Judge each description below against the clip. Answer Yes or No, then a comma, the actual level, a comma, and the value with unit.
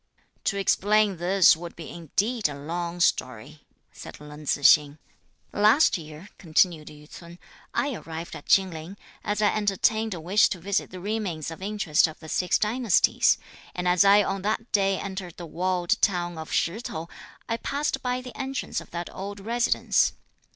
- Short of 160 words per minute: No, average, 175 wpm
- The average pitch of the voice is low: No, medium, 185 Hz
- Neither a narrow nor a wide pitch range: Yes, average, 4.2 semitones